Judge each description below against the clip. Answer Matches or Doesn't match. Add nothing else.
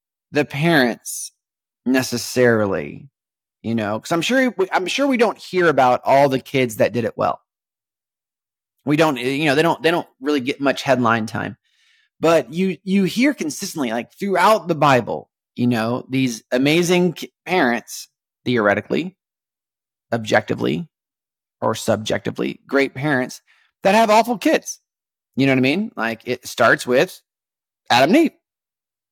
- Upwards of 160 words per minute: Doesn't match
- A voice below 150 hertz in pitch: Matches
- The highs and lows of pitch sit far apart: Matches